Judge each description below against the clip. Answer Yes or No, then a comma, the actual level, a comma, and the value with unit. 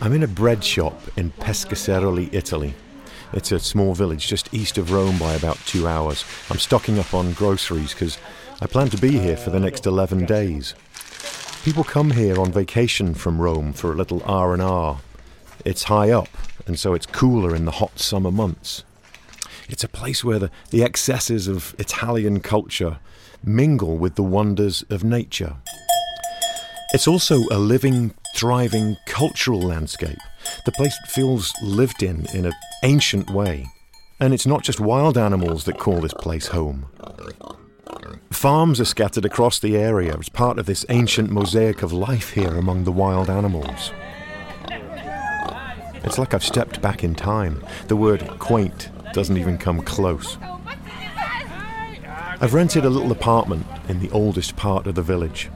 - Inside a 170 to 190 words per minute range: No, average, 160 wpm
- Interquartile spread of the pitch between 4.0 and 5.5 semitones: Yes, average, 4.7 semitones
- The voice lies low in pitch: Yes, low, 100 Hz